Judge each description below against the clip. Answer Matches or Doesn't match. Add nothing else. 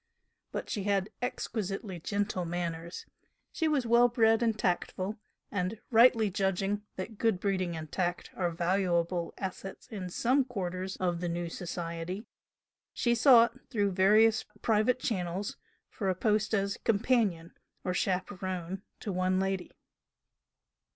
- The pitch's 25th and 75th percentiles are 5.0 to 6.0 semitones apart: Doesn't match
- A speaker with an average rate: Doesn't match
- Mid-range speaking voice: Doesn't match